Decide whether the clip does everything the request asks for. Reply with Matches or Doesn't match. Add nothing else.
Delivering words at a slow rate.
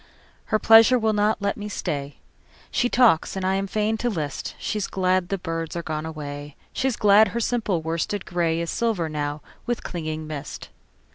Doesn't match